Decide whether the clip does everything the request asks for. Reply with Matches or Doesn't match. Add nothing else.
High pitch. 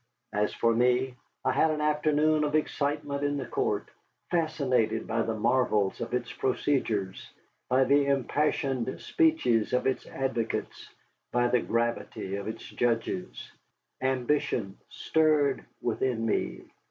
Doesn't match